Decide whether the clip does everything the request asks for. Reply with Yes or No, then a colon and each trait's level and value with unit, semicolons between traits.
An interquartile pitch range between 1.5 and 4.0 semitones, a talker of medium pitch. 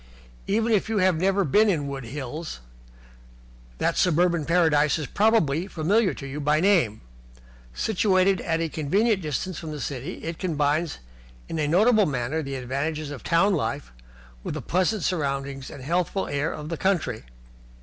No: average, 4.6 semitones; medium, 160 Hz